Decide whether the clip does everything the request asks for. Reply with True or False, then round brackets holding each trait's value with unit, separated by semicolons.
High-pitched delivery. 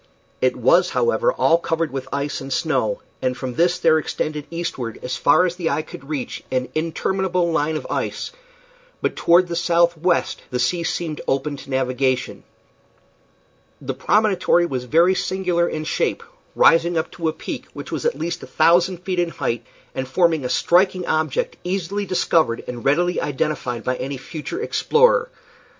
False (165 Hz)